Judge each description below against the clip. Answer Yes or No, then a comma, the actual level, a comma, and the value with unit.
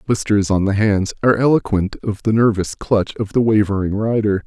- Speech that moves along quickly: No, average, 190 wpm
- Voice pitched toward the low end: Yes, low, 105 Hz